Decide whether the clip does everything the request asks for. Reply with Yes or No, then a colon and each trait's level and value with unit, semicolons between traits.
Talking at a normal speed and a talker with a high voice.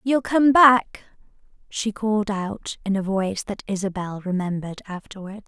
Yes: average, 145 wpm; high, 205 Hz